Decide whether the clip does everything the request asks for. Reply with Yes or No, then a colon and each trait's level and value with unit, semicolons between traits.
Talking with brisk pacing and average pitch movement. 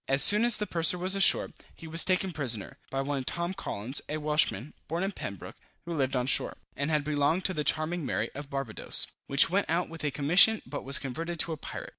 Yes: fast, 225 wpm; average, 4.2 semitones